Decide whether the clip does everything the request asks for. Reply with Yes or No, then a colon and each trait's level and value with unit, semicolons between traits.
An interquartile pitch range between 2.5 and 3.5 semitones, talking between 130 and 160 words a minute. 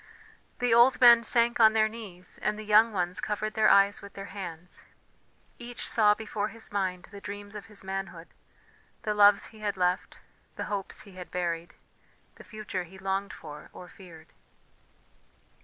No: average, 2.8 semitones; average, 170 wpm